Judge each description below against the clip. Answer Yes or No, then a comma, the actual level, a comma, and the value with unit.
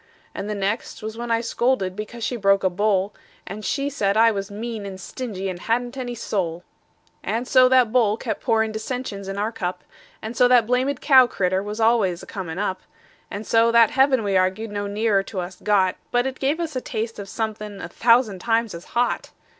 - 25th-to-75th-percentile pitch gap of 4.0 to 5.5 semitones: No, average, 3.4 semitones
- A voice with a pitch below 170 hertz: No, high, 220 Hz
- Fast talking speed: Yes, fast, 210 wpm